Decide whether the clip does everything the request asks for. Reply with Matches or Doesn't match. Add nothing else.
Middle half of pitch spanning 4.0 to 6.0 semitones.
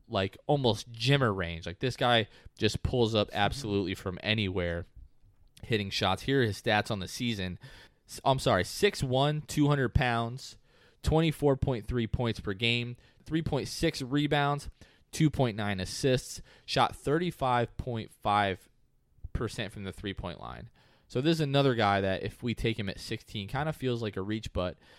Matches